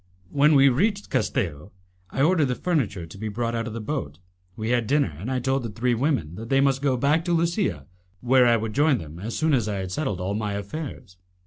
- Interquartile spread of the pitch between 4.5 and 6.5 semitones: Yes, wide, 5.6 semitones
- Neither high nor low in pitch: No, low, 120 Hz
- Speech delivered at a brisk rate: Yes, fast, 235 wpm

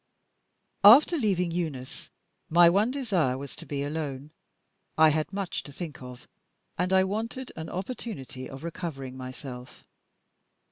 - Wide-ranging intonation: Yes, wide, 6.2 semitones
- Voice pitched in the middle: Yes, medium, 165 Hz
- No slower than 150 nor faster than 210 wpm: No, slow, 135 wpm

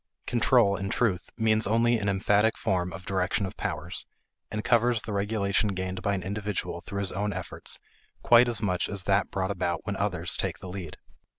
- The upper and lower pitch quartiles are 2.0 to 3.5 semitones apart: Yes, narrow, 2.5 semitones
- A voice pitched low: Yes, low, 100 Hz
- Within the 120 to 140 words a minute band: No, average, 190 wpm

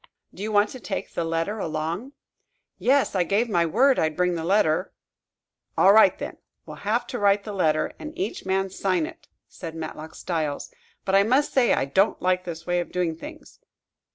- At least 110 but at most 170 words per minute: No, average, 195 wpm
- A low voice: No, high, 190 Hz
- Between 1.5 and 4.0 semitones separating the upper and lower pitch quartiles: No, average, 4.4 semitones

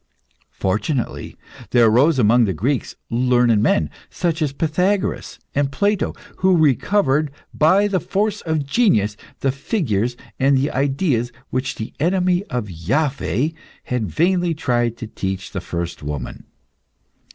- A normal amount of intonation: No, wide, 6.5 semitones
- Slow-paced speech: Yes, slow, 130 wpm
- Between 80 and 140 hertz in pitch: Yes, low, 135 Hz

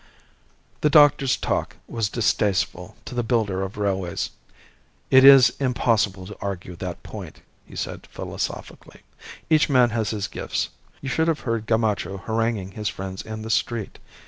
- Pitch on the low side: Yes, low, 110 Hz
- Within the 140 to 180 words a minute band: Yes, average, 150 wpm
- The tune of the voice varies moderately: Yes, average, 4.1 semitones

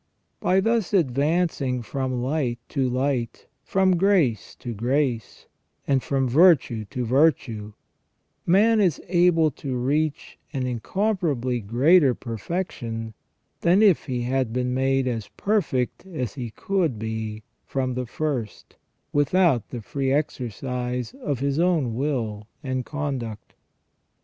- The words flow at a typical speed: No, slow, 125 wpm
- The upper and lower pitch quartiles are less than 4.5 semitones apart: No, average, 4.9 semitones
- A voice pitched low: Yes, low, 130 Hz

